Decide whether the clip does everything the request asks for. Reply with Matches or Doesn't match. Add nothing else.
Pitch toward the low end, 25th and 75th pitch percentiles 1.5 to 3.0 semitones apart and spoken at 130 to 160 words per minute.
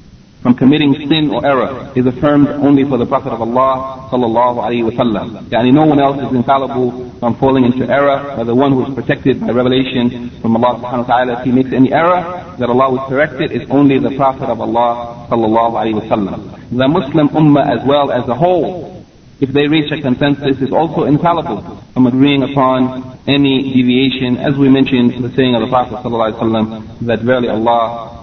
Doesn't match